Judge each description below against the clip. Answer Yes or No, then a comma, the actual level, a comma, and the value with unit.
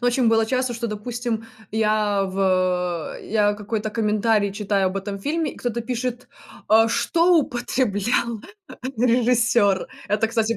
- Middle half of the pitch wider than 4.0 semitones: No, average, 2.9 semitones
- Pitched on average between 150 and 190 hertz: No, high, 225 Hz